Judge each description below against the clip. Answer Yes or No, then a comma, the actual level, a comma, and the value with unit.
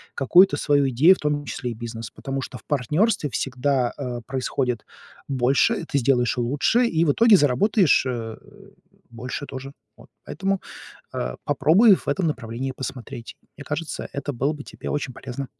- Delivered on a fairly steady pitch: No, average, 3.2 semitones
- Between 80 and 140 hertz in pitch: Yes, low, 135 Hz